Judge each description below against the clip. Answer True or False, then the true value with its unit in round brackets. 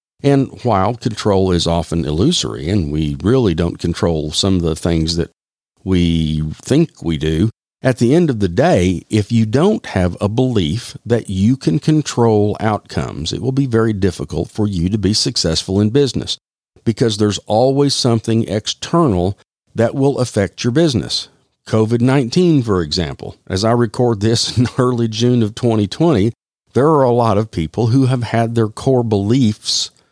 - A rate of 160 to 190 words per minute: True (165 wpm)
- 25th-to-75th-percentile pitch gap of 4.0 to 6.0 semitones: True (5.3 semitones)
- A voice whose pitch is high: False (110 Hz)